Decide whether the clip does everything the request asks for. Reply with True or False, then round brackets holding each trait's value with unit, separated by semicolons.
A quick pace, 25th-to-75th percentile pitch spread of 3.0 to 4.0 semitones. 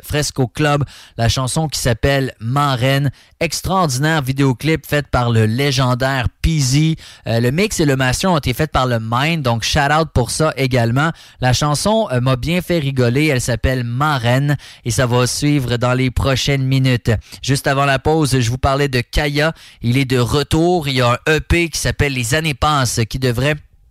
False (190 wpm; 3.4 semitones)